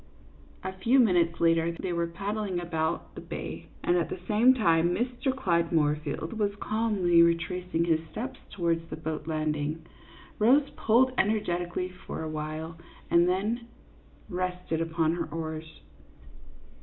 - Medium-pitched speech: Yes, medium, 175 Hz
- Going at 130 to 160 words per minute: Yes, average, 140 wpm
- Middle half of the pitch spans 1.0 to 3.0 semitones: No, average, 4.2 semitones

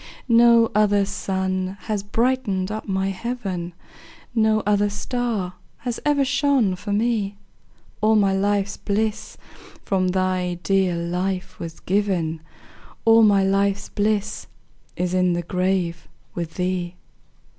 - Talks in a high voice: Yes, high, 195 Hz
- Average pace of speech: No, slow, 125 wpm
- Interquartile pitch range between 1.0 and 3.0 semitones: Yes, average, 2.7 semitones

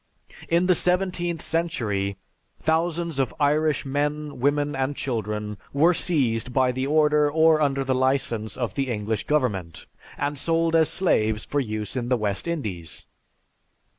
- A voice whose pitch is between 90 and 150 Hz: Yes, medium, 140 Hz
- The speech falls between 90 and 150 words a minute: Yes, average, 145 wpm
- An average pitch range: No, wide, 5.7 semitones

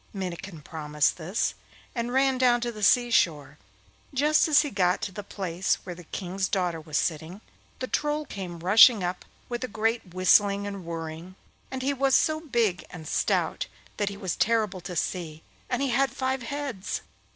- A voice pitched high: Yes, high, 200 Hz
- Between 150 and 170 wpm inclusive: No, average, 180 wpm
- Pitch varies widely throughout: Yes, wide, 5.8 semitones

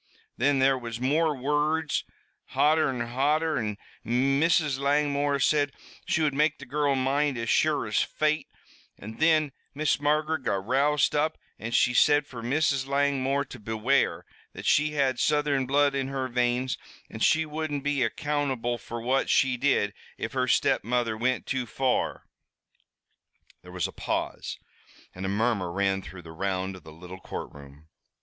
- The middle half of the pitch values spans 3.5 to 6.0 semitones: Yes, average, 3.8 semitones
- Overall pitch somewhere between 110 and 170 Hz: Yes, low, 135 Hz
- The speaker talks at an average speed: Yes, average, 155 wpm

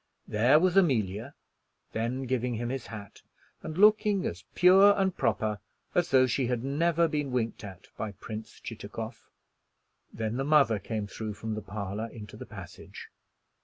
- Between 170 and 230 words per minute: No, average, 160 wpm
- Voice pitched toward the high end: No, low, 120 Hz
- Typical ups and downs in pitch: No, wide, 6.0 semitones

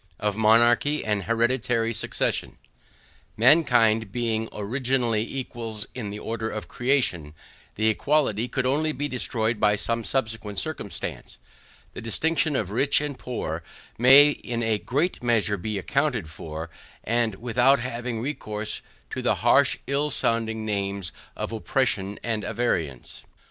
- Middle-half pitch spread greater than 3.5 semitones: No, average, 3.2 semitones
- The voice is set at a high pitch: No, low, 115 Hz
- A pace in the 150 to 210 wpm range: No, slow, 135 wpm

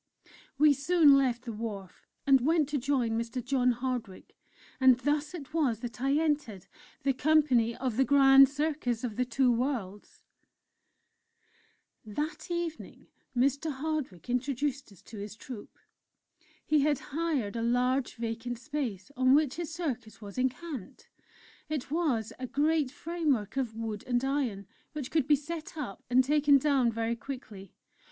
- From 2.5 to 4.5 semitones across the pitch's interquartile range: Yes, average, 4.0 semitones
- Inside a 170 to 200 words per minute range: No, average, 150 wpm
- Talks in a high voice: Yes, very high, 260 Hz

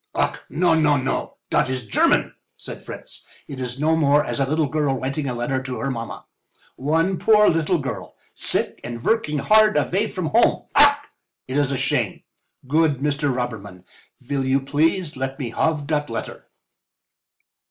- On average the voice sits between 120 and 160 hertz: Yes, medium, 140 Hz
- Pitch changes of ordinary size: Yes, average, 3.4 semitones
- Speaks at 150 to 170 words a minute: Yes, average, 165 wpm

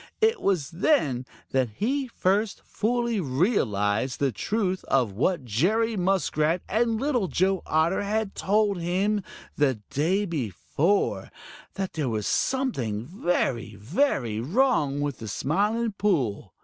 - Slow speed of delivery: Yes, slow, 125 wpm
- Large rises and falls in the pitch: Yes, wide, 8.2 semitones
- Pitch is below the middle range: No, medium, 180 Hz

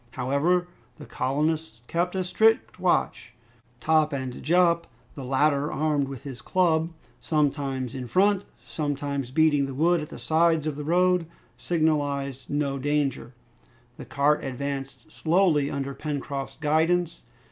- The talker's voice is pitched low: No, medium, 150 Hz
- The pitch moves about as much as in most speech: Yes, average, 3.3 semitones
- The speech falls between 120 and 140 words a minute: Yes, slow, 135 wpm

